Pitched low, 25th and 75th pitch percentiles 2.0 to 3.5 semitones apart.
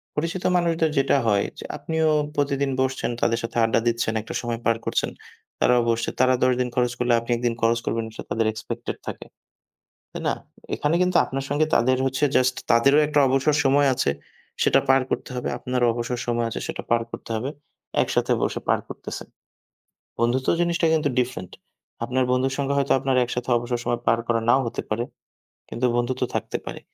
Yes: low, 125 Hz; average, 2.8 semitones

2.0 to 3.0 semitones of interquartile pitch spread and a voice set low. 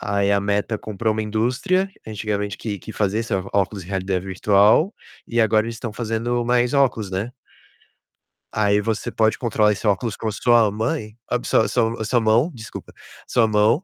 Yes: narrow, 2.5 semitones; low, 110 Hz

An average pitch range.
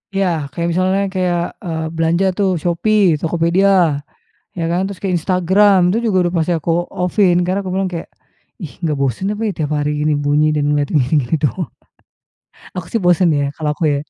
Yes: average, 3.5 semitones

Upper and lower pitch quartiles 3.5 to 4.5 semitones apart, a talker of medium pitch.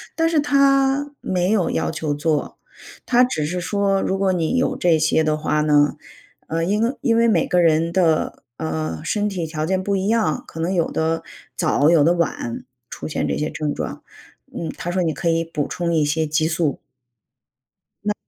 Yes: average, 4.2 semitones; medium, 165 Hz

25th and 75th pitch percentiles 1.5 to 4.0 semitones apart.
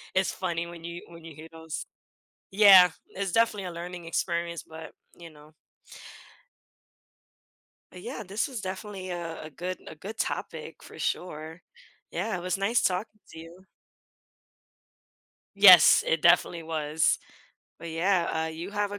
Yes: average, 2.8 semitones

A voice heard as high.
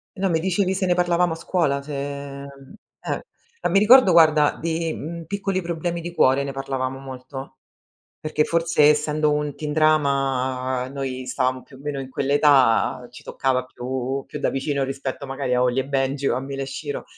No: medium, 140 Hz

